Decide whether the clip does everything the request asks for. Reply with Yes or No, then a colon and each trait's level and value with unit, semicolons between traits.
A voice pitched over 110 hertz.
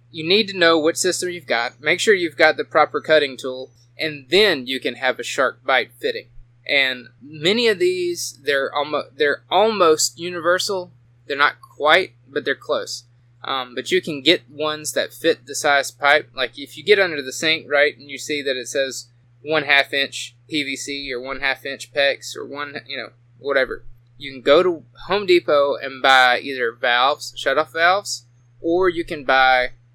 Yes: medium, 140 Hz